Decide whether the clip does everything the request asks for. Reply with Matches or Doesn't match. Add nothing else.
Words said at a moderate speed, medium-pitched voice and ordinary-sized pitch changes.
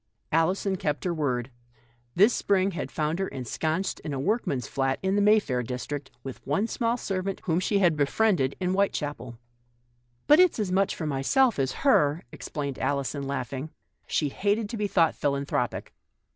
Doesn't match